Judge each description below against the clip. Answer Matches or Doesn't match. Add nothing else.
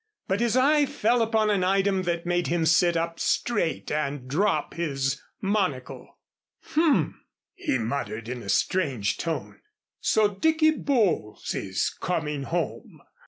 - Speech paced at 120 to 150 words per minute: Matches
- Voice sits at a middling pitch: Matches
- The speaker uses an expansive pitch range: Matches